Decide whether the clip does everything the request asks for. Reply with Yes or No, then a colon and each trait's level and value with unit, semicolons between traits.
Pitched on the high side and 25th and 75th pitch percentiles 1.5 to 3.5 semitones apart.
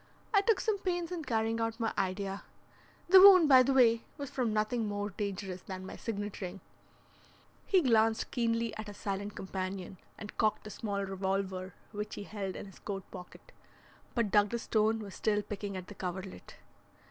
Yes: high, 210 Hz; average, 3.1 semitones